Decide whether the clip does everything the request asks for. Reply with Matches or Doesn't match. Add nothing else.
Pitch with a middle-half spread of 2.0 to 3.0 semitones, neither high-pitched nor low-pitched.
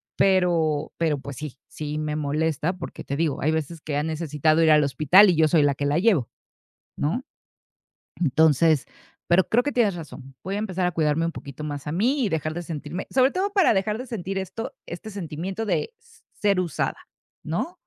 Doesn't match